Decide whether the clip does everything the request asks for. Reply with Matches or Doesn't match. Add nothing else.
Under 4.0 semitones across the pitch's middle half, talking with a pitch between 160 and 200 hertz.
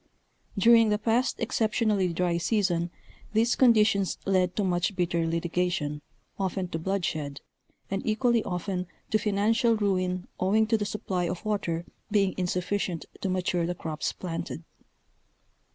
Matches